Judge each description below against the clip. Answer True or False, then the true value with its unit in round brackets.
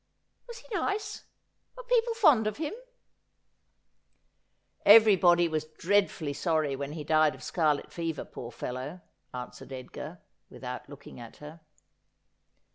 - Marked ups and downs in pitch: True (7.1 semitones)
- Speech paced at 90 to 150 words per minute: True (140 wpm)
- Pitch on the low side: False (165 Hz)